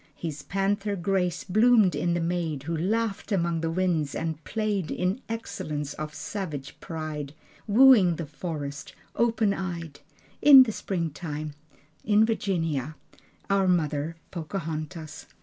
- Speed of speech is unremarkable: No, slow, 125 wpm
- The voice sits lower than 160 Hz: No, medium, 170 Hz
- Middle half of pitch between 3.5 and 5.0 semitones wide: Yes, average, 4.4 semitones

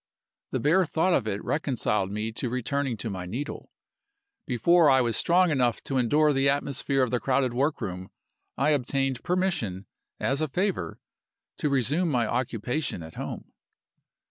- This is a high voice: No, low, 135 Hz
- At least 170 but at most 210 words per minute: No, average, 155 wpm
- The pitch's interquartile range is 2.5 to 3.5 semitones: No, average, 4.5 semitones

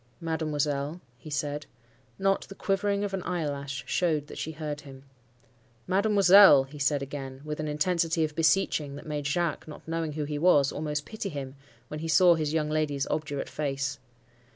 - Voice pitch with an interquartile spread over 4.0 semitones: No, narrow, 2.6 semitones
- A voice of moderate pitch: Yes, medium, 150 Hz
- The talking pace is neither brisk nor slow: Yes, average, 165 wpm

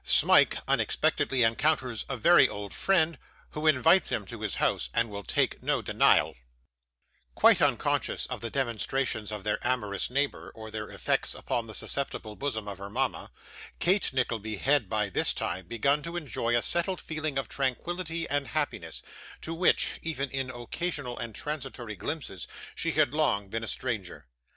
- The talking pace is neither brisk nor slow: Yes, average, 165 wpm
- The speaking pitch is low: Yes, low, 130 Hz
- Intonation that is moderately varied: No, wide, 5.8 semitones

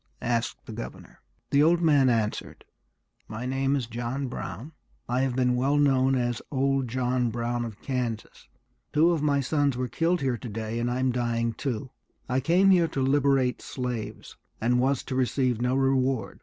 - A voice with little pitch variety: Yes, narrow, 2.3 semitones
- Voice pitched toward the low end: Yes, low, 130 Hz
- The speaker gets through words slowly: No, average, 175 wpm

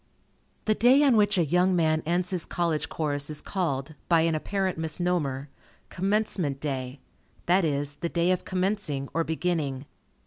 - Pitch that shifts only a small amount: No, average, 4.0 semitones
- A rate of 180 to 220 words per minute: No, average, 160 wpm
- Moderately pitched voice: Yes, medium, 170 Hz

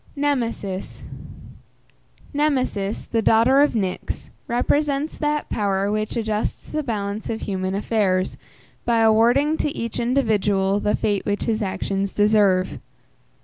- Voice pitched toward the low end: No, high, 220 Hz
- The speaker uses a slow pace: Yes, slow, 120 wpm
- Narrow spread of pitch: No, average, 4.2 semitones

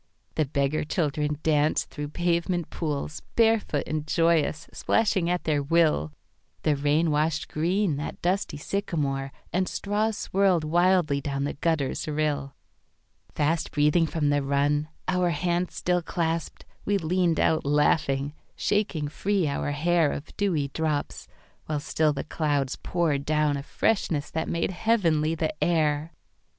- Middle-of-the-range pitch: Yes, medium, 155 Hz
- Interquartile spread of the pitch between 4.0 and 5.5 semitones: No, average, 3.0 semitones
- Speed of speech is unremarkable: No, slow, 125 wpm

